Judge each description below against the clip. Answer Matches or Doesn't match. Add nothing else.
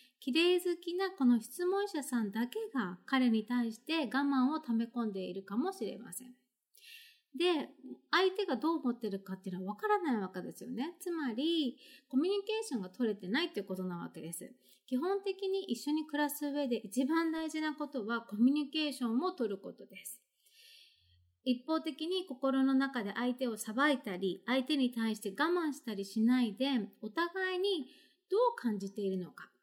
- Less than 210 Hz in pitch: Doesn't match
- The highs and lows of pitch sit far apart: Matches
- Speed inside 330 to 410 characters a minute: Matches